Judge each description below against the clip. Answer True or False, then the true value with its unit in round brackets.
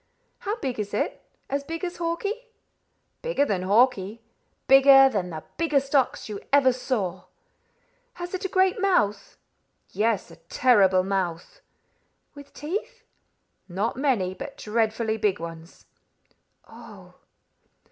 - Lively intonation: True (7.4 semitones)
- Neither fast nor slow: False (125 wpm)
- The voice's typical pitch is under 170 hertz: False (250 Hz)